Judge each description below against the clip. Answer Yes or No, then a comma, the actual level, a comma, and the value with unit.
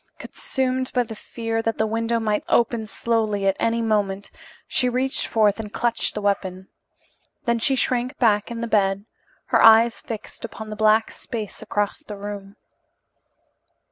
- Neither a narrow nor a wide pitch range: No, narrow, 2.2 semitones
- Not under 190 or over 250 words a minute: No, average, 160 wpm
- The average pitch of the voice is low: No, high, 220 Hz